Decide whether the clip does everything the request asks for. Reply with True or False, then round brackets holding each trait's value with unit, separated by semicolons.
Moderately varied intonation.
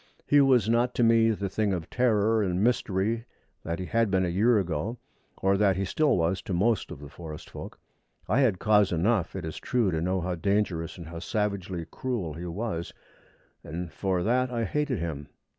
True (4.7 semitones)